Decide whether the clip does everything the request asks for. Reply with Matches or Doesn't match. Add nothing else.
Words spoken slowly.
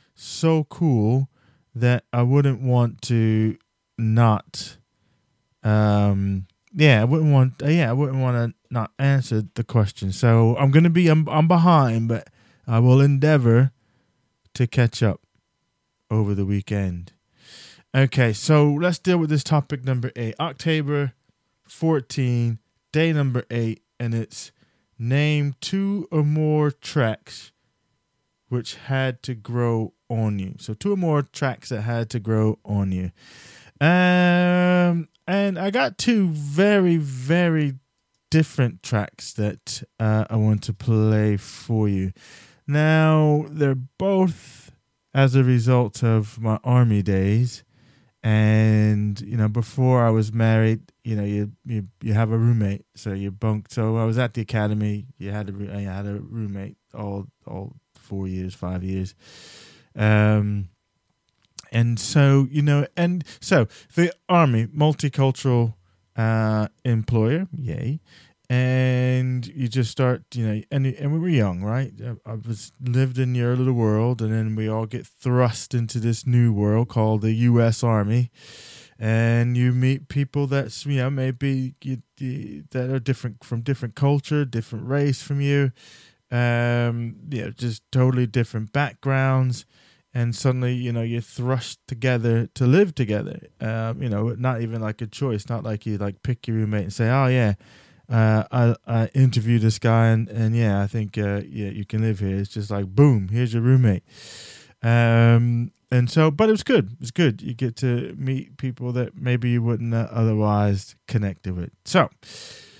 Doesn't match